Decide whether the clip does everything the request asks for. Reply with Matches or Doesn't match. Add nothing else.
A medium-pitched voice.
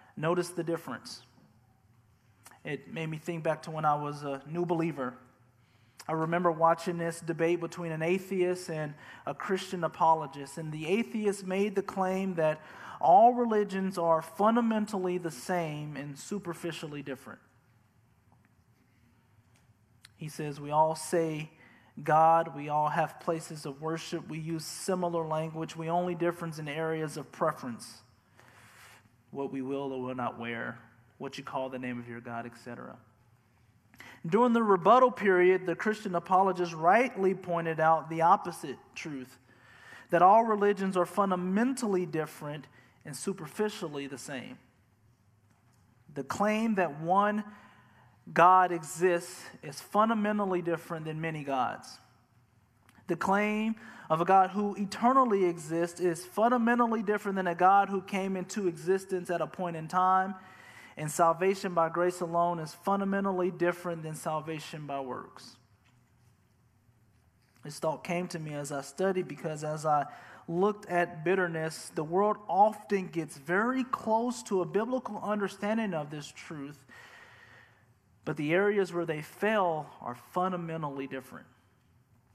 Matches